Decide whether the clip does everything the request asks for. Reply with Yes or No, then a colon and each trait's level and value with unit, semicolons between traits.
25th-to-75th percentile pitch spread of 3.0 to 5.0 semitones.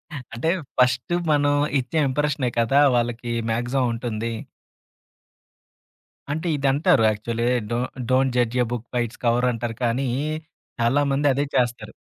No: narrow, 2.6 semitones